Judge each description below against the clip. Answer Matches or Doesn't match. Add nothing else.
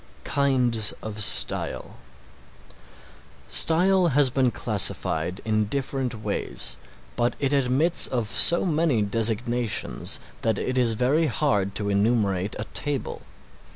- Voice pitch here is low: Matches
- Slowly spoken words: Matches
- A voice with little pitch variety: Doesn't match